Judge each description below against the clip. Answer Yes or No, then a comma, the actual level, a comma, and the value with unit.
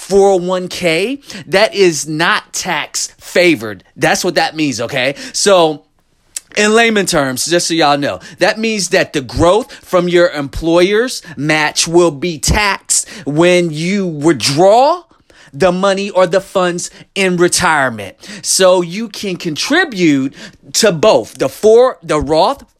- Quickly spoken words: No, slow, 135 wpm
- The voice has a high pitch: No, medium, 180 Hz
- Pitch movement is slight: No, average, 4.0 semitones